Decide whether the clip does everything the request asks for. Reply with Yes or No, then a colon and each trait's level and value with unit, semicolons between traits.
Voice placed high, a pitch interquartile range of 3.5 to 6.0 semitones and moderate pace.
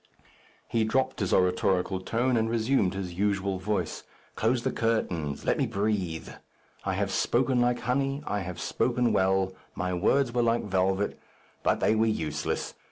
No: low, 105 Hz; average, 4.1 semitones; average, 160 wpm